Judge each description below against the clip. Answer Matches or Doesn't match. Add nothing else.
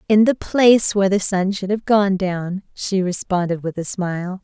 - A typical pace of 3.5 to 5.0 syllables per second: Matches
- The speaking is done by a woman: Matches